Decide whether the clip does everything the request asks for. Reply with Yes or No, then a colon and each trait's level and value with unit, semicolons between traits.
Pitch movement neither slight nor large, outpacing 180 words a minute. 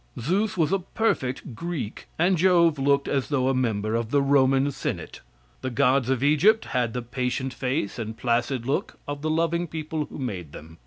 Yes: average, 4.4 semitones; average, 190 wpm